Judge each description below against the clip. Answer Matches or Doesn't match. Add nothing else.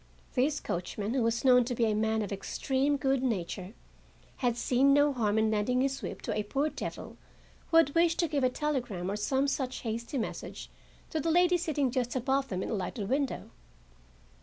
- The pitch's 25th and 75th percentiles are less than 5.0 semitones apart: Matches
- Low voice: Doesn't match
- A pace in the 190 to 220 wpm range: Matches